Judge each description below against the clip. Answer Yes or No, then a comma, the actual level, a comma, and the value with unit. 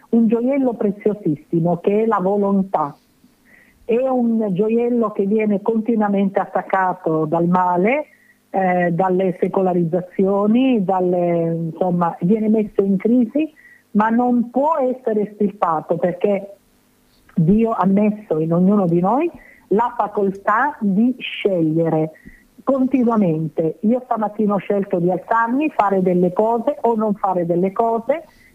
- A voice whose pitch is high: Yes, high, 205 Hz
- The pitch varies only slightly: No, average, 4.2 semitones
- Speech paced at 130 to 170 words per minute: No, average, 120 wpm